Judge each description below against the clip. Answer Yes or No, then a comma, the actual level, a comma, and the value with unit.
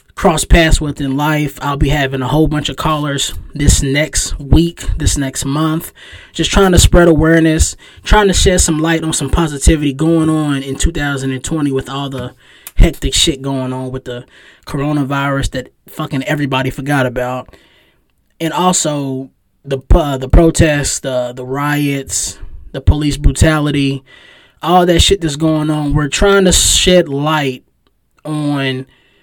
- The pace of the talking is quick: No, average, 155 wpm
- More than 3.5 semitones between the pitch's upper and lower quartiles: No, average, 3.0 semitones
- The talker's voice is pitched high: No, medium, 140 Hz